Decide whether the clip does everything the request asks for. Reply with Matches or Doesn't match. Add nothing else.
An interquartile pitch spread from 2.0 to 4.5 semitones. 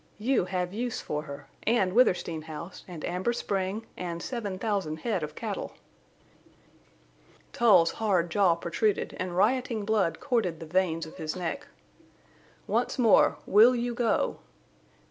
Doesn't match